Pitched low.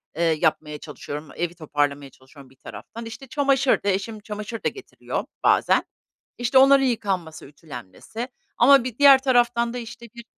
No: high, 220 Hz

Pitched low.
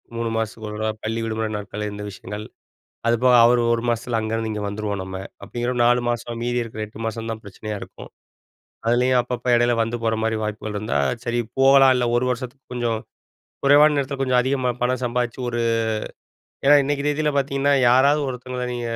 Yes: low, 120 Hz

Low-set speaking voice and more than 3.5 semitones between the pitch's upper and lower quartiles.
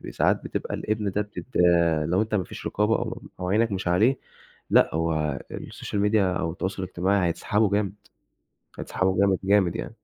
No: low, 100 Hz; narrow, 2.6 semitones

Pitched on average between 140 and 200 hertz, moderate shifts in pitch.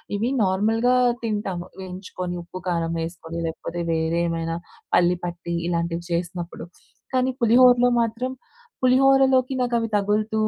No: high, 190 Hz; wide, 5.9 semitones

